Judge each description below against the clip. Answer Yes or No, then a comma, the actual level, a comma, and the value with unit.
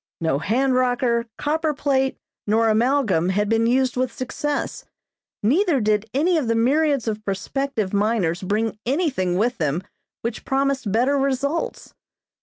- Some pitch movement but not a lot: Yes, average, 4.6 semitones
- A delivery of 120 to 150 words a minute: Yes, average, 140 wpm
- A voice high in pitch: Yes, high, 240 Hz